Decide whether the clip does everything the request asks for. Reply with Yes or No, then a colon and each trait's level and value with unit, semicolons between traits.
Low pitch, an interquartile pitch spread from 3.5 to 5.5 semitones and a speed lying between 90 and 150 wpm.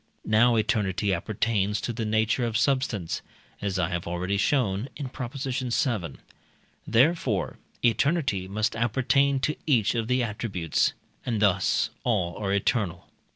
Yes: low, 110 Hz; average, 4.2 semitones; slow, 135 wpm